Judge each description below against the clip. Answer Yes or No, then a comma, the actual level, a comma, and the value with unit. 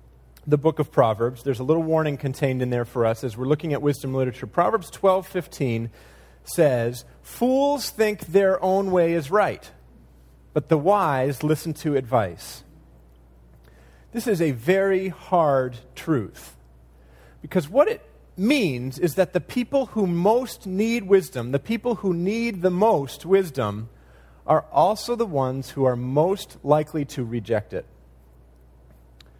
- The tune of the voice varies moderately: No, wide, 8.5 semitones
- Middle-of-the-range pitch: Yes, medium, 145 Hz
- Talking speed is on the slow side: No, average, 145 wpm